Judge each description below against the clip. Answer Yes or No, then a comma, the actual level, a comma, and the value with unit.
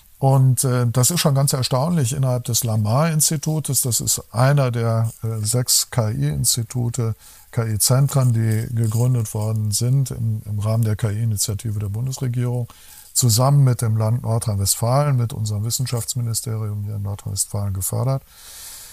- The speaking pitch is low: Yes, low, 120 Hz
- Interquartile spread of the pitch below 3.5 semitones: Yes, average, 2.8 semitones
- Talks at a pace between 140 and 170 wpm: No, average, 130 wpm